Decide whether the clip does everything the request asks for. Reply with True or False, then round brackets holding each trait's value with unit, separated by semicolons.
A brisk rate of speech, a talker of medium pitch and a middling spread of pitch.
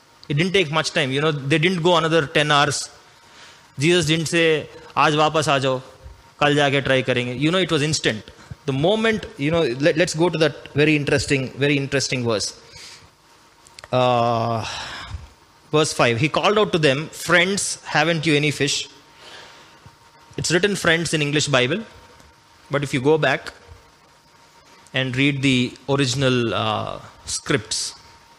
True (145 wpm; 150 Hz; 3.4 semitones)